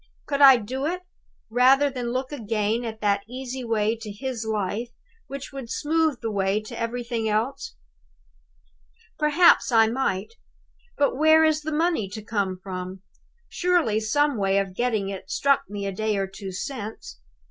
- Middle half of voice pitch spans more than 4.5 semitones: Yes, average, 4.9 semitones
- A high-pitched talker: Yes, high, 230 Hz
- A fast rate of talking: No, average, 160 wpm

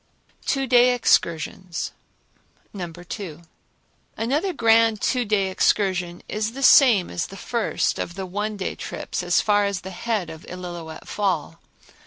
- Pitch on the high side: Yes, high, 200 Hz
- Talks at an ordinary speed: Yes, average, 145 wpm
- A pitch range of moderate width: Yes, average, 4.4 semitones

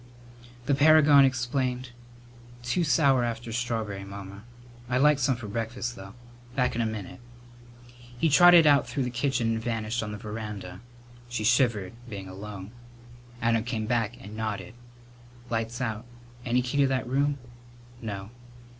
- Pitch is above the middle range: No, low, 120 Hz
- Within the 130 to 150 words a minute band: Yes, average, 145 wpm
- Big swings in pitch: No, average, 3.3 semitones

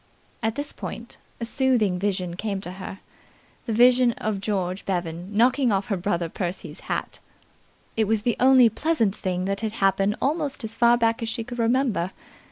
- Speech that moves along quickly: No, average, 175 wpm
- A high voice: Yes, high, 215 Hz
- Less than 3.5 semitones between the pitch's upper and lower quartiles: No, average, 3.8 semitones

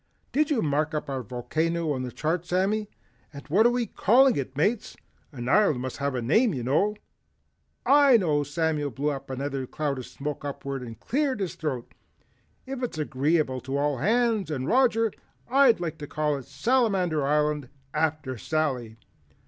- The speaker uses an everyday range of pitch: No, wide, 7.4 semitones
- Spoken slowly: No, average, 170 wpm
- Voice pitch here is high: No, medium, 155 Hz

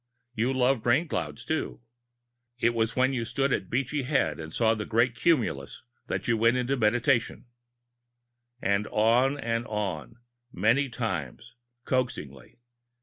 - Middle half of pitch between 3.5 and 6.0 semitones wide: No, average, 2.9 semitones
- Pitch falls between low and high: No, low, 120 Hz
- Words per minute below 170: Yes, average, 140 wpm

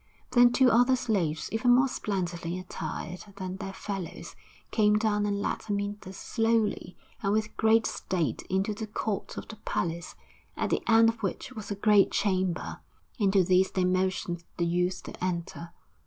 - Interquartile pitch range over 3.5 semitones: No, average, 3.2 semitones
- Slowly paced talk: No, average, 165 wpm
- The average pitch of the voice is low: No, high, 200 Hz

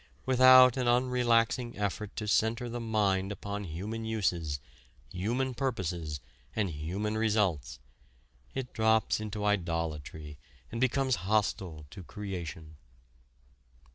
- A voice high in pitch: No, low, 105 Hz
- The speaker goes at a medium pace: No, slow, 110 wpm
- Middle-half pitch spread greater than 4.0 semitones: Yes, average, 5.2 semitones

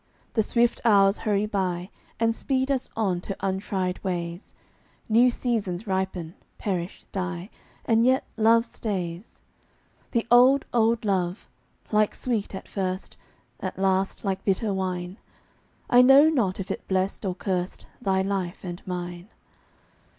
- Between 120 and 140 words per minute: Yes, slow, 135 wpm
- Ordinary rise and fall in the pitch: Yes, average, 3.6 semitones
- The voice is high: Yes, high, 195 Hz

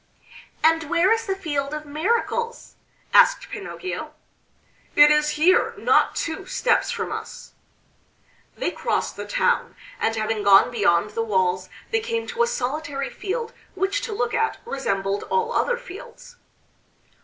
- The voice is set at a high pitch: Yes, very high, 325 Hz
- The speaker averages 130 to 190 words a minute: Yes, average, 145 wpm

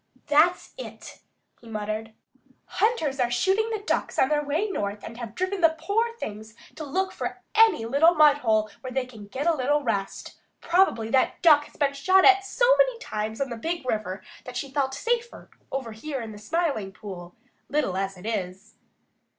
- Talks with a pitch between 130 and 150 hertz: No, very high, 275 Hz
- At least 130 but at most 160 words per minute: No, average, 185 wpm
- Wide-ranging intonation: Yes, wide, 7.7 semitones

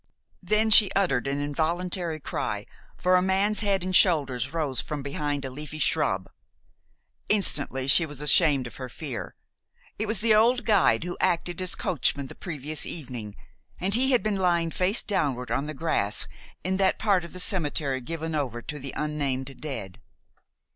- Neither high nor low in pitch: Yes, medium, 160 Hz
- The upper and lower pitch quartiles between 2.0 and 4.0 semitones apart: No, average, 5.2 semitones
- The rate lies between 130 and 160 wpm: No, average, 170 wpm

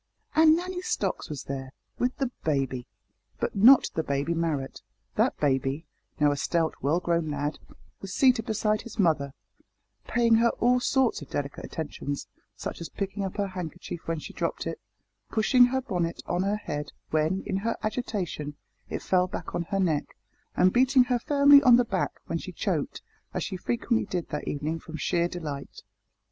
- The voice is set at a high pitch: No, medium, 180 Hz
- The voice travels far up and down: Yes, wide, 7.5 semitones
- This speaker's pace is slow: No, average, 180 wpm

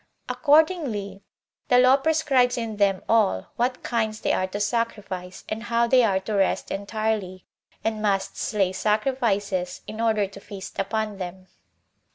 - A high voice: Yes, high, 215 Hz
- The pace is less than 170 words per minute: Yes, average, 150 wpm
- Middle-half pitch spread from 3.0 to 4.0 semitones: Yes, average, 3.3 semitones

